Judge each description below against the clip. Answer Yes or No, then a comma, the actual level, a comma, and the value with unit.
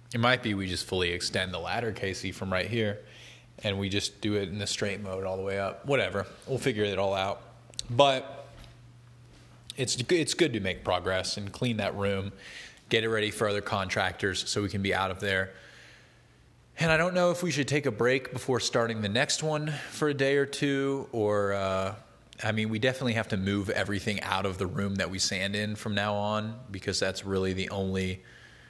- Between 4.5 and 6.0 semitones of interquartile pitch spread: No, average, 4.0 semitones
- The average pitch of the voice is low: Yes, low, 105 Hz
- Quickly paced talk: Yes, fast, 215 wpm